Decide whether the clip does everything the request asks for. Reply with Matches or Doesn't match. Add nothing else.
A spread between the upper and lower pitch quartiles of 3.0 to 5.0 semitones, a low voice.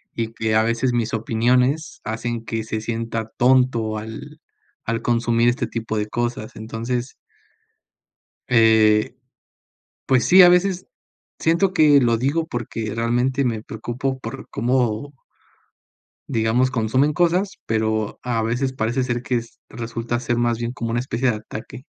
Doesn't match